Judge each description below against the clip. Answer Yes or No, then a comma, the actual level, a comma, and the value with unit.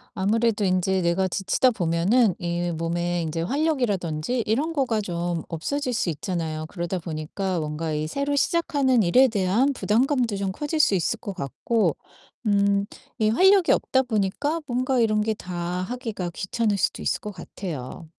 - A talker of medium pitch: No, high, 200 Hz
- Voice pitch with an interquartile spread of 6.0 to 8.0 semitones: Yes, wide, 6.3 semitones